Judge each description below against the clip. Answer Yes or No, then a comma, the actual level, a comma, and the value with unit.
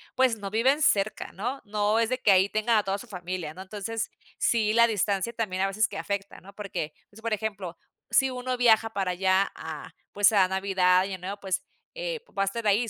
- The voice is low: No, high, 205 Hz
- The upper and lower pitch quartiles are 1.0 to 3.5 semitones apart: Yes, average, 3.0 semitones